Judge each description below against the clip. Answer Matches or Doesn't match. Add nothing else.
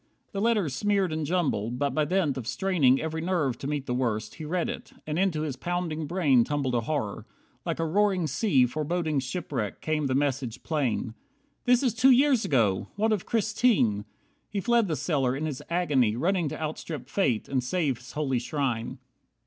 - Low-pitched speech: Doesn't match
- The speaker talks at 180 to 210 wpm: Matches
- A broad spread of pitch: Matches